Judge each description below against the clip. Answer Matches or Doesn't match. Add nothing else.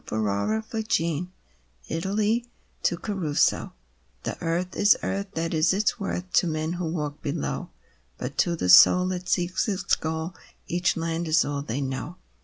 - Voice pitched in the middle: Matches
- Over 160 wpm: Matches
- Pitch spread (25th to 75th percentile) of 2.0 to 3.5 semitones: Matches